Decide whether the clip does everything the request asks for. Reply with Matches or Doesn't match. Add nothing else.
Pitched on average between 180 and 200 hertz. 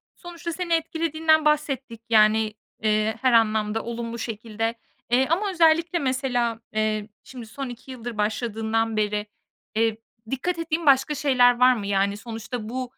Doesn't match